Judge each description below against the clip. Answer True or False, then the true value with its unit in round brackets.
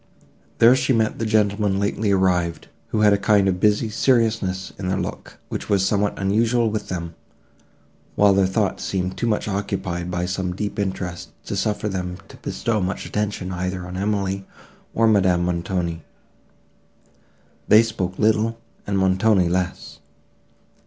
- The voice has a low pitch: True (100 Hz)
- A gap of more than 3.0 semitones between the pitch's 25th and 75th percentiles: False (2.6 semitones)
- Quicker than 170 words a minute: False (150 wpm)